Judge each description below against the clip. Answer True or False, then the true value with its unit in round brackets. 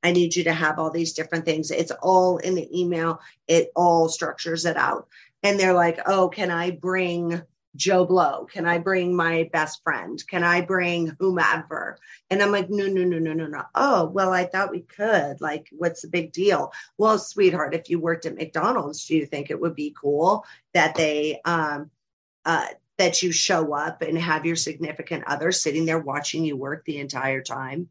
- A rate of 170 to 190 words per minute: False (200 wpm)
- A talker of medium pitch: True (170 Hz)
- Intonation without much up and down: True (2.3 semitones)